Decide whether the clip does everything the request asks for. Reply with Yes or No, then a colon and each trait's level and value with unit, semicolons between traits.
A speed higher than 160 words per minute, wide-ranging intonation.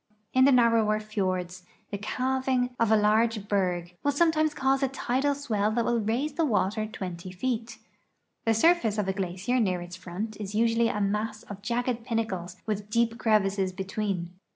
No: average, 175 wpm; average, 3.8 semitones